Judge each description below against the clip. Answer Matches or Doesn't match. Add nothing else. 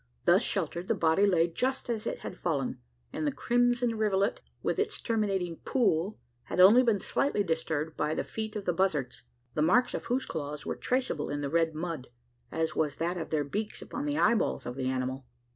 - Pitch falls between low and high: Matches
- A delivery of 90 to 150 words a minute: Doesn't match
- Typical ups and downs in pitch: Doesn't match